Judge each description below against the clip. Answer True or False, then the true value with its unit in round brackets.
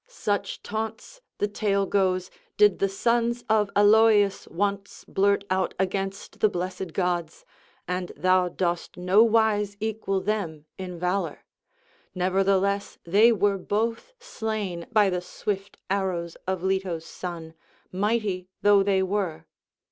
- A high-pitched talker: True (195 Hz)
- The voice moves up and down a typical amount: False (2.3 semitones)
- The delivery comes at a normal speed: False (125 wpm)